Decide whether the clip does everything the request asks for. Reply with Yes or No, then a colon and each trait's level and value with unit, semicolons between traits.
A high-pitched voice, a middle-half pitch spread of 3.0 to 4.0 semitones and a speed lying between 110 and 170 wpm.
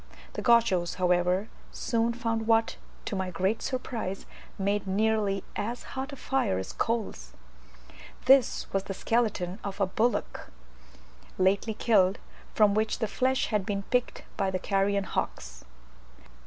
Yes: high, 205 Hz; average, 3.4 semitones; average, 140 wpm